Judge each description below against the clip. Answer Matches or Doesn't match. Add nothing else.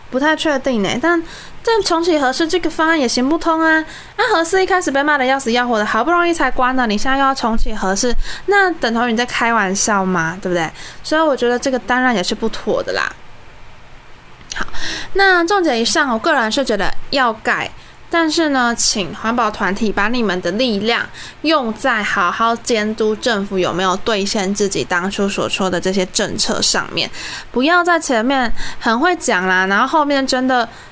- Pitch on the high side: Matches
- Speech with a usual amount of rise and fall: Doesn't match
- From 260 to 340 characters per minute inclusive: Matches